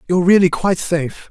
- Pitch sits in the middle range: Yes, medium, 175 Hz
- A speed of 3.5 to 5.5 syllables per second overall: No, 7.1 syllables/s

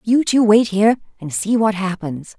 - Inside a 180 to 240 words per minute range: Yes, average, 200 wpm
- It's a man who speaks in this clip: No, female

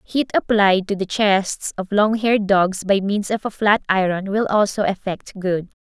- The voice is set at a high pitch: Yes, high, 200 Hz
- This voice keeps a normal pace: Yes, average, 195 wpm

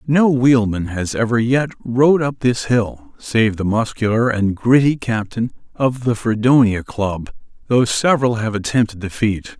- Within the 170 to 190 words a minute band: No, average, 155 wpm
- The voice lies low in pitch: Yes, low, 115 Hz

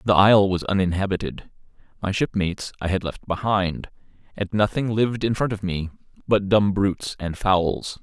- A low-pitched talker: Yes, low, 100 Hz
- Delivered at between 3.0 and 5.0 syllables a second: No, 5.2 syllables/s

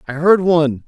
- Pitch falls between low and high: Yes, medium, 160 Hz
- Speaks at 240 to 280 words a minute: No, fast, 205 wpm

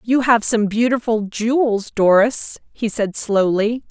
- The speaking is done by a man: No, female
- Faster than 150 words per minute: No, average, 140 wpm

